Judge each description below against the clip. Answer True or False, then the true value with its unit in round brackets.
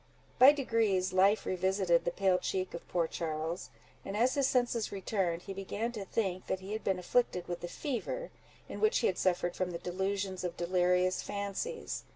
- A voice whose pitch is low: False (190 Hz)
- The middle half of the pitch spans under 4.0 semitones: True (3.4 semitones)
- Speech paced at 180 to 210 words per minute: True (190 wpm)